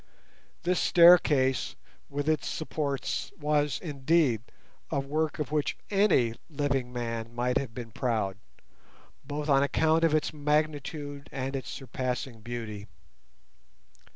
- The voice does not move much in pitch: No, average, 3.6 semitones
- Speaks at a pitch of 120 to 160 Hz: Yes, medium, 140 Hz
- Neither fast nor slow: No, slow, 120 wpm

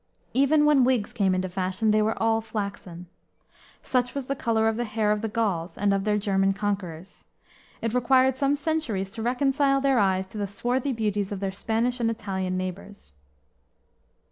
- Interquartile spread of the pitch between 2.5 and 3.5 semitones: No, average, 4.2 semitones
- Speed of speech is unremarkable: Yes, average, 180 wpm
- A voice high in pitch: Yes, high, 220 Hz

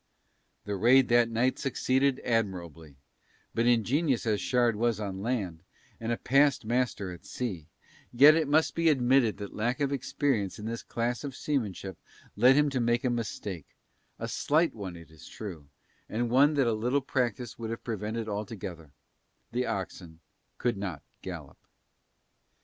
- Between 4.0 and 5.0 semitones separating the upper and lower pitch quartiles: Yes, average, 4.3 semitones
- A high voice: No, low, 115 Hz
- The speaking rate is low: No, average, 160 wpm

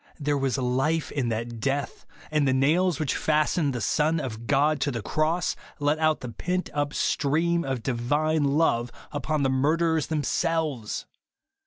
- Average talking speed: Yes, average, 160 wpm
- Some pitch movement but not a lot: Yes, average, 3.1 semitones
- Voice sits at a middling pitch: Yes, medium, 145 Hz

